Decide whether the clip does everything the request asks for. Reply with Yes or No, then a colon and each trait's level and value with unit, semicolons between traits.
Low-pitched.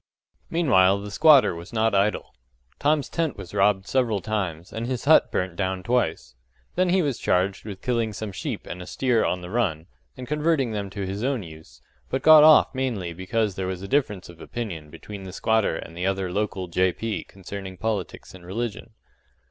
Yes: low, 100 Hz